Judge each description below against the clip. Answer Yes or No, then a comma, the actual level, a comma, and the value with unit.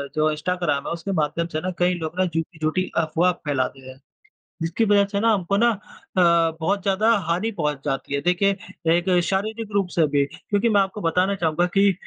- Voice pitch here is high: No, medium, 175 Hz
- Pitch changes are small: No, average, 4.0 semitones